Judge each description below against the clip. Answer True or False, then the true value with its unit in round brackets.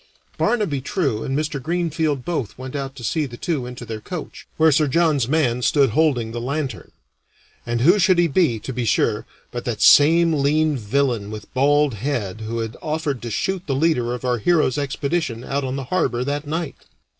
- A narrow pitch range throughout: False (4.5 semitones)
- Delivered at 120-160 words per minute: False (195 wpm)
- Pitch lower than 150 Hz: True (140 Hz)